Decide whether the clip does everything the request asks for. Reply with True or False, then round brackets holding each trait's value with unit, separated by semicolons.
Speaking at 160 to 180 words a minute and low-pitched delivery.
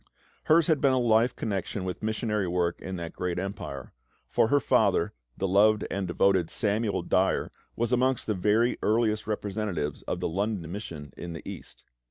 True (175 wpm; 105 Hz)